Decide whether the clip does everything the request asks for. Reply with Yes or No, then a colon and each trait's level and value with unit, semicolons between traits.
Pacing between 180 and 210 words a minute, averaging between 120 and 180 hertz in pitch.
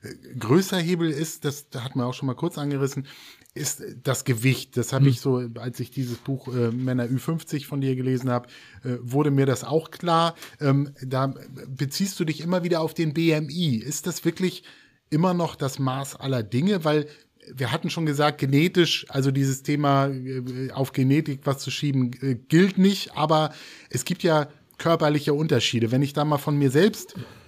Yes: average, 185 wpm; medium, 140 Hz